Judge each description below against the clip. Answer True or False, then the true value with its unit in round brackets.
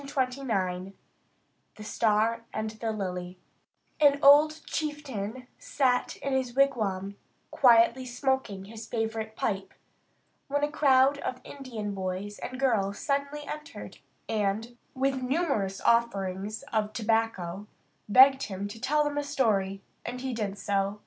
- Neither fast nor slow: False (130 wpm)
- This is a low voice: False (230 Hz)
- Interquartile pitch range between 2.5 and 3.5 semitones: False (5.0 semitones)